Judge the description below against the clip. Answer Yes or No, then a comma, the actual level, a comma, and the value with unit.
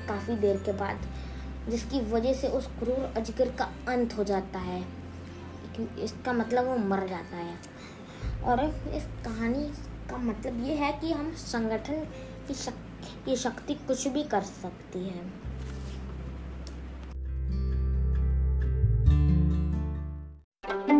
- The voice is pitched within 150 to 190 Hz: Yes, medium, 185 Hz